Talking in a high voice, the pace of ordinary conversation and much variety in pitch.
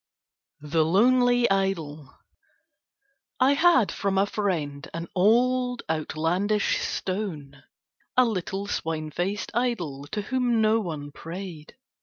No: high, 195 Hz; slow, 110 wpm; wide, 6.5 semitones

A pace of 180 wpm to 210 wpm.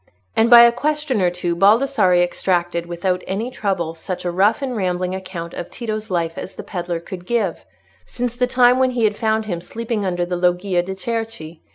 Yes: average, 200 wpm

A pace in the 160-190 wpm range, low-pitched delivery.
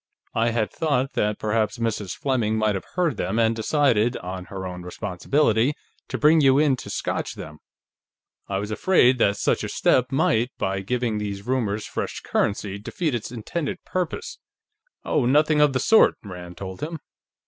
Yes: average, 170 wpm; low, 115 Hz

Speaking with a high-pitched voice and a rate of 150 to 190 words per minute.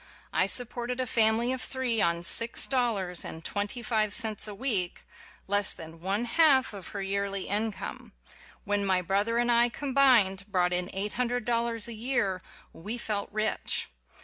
Yes: high, 215 Hz; average, 170 wpm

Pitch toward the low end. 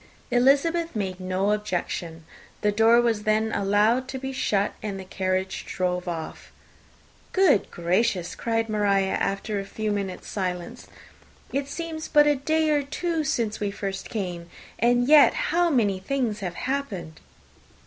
No: high, 215 Hz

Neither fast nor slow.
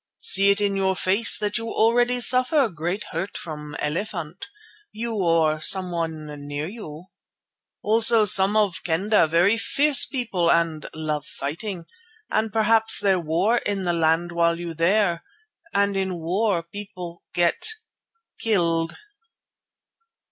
No: slow, 130 wpm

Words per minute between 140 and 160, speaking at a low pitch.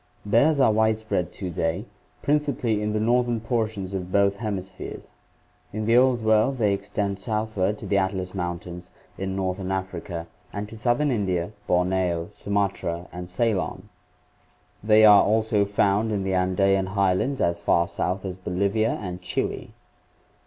Yes: average, 150 wpm; low, 100 Hz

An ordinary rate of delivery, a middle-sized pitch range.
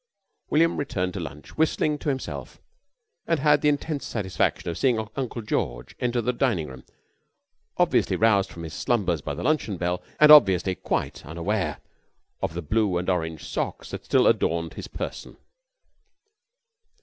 No: average, 155 wpm; wide, 7.9 semitones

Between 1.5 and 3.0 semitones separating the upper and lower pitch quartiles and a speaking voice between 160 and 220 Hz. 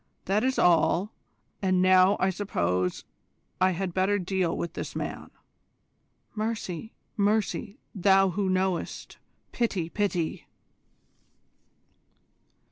Yes: narrow, 2.4 semitones; high, 190 Hz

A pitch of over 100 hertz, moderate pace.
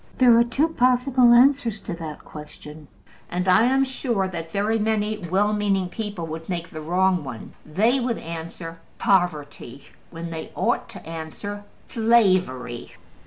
Yes: high, 190 Hz; average, 150 wpm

